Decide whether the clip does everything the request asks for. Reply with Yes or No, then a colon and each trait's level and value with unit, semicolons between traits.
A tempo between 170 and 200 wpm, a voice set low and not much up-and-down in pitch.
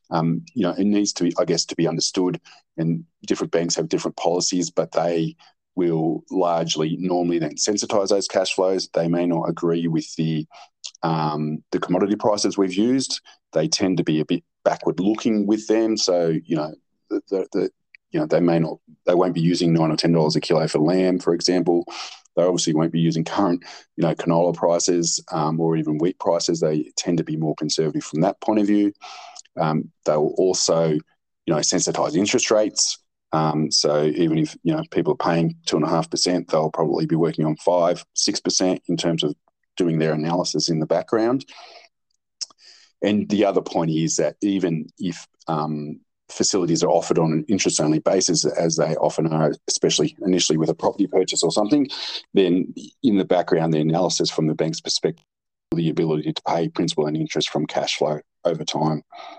Yes: average, 190 wpm; very low, 85 Hz; narrow, 2.3 semitones